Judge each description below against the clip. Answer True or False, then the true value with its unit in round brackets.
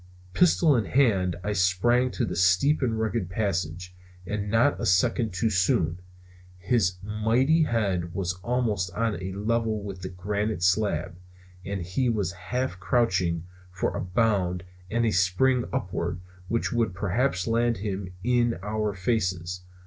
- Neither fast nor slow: True (150 wpm)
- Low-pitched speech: True (100 Hz)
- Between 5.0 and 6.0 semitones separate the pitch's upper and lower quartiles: False (4.2 semitones)